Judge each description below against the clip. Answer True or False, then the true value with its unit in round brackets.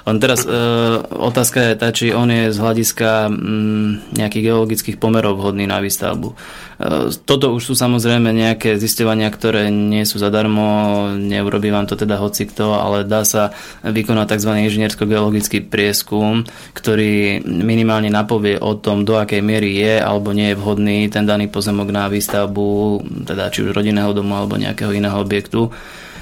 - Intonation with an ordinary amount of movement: False (1.5 semitones)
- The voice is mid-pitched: False (105 Hz)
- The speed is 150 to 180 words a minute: True (160 wpm)